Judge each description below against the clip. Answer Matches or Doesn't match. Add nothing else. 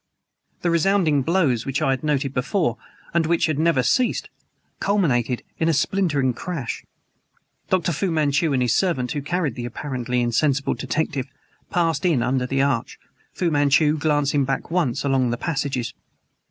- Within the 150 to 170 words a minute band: Matches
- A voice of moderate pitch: Matches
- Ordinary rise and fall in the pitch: Matches